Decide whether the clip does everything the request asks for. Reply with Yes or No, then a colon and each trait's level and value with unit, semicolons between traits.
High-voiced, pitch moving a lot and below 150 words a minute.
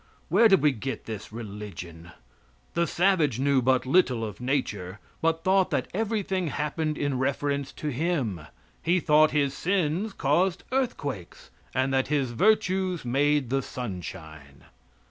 No: medium, 140 Hz; wide, 6.5 semitones; average, 140 wpm